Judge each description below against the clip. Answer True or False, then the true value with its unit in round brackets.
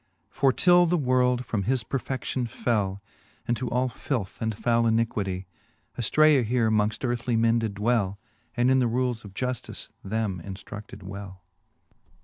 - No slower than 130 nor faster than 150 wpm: True (145 wpm)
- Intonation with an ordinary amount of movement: True (3.4 semitones)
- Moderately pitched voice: False (115 Hz)